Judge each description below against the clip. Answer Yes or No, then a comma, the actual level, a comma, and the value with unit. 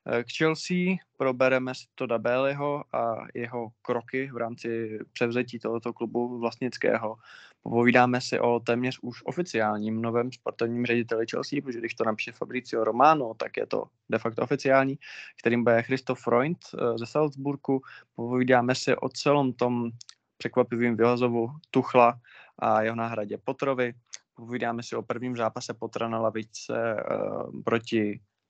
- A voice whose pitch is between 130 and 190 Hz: No, low, 120 Hz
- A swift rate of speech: No, average, 135 wpm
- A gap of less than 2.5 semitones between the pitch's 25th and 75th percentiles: Yes, narrow, 2.0 semitones